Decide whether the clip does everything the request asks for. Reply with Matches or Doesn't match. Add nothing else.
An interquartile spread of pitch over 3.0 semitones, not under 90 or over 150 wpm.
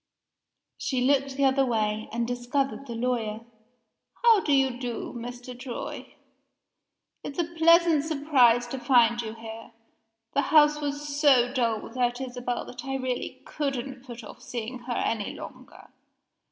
Doesn't match